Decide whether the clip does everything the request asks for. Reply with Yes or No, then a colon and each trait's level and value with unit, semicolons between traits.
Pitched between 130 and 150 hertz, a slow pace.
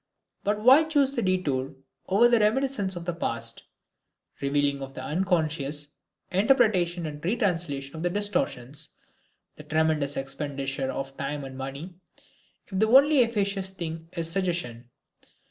No: medium, 170 Hz; slow, 130 wpm